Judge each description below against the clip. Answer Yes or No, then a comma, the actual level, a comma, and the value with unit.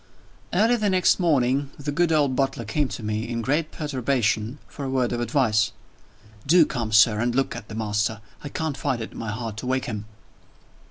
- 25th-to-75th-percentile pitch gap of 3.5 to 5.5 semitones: Yes, average, 4.6 semitones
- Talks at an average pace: No, fast, 210 wpm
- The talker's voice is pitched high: No, low, 125 Hz